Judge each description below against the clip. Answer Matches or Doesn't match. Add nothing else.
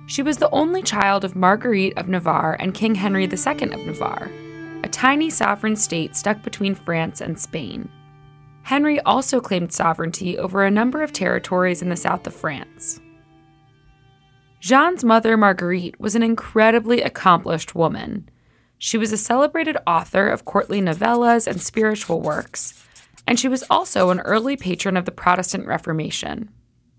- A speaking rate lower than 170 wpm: Matches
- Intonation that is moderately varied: Doesn't match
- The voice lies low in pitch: Doesn't match